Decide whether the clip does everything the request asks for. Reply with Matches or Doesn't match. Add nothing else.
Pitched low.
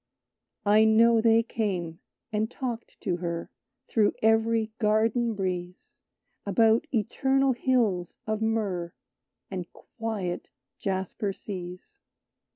Doesn't match